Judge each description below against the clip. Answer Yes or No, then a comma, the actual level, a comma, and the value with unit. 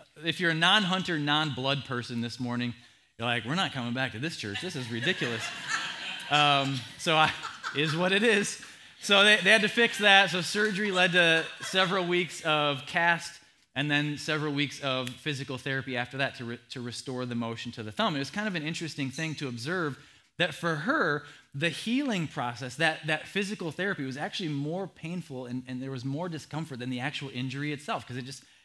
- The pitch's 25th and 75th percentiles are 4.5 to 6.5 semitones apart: Yes, average, 5.1 semitones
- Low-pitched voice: No, medium, 150 Hz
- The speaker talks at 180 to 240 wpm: Yes, fast, 205 wpm